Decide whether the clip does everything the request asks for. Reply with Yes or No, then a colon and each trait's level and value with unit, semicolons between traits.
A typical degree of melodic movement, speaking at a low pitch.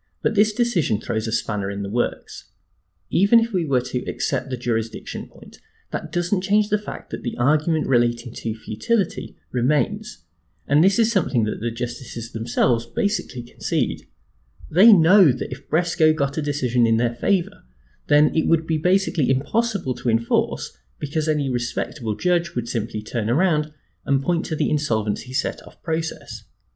No: wide, 6.5 semitones; low, 130 Hz